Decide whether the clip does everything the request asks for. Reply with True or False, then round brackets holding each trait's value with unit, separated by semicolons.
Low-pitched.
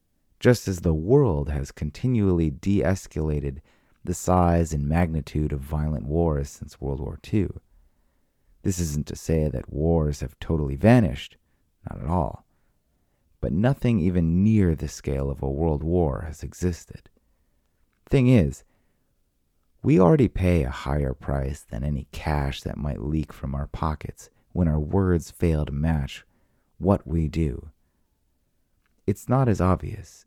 True (80 Hz)